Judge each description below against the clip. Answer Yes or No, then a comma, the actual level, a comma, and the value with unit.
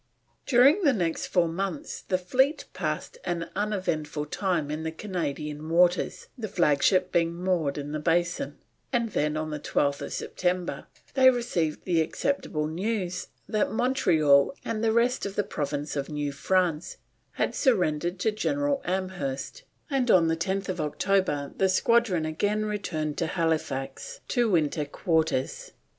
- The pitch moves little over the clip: No, wide, 5.4 semitones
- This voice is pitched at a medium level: Yes, medium, 175 Hz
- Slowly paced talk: No, average, 145 wpm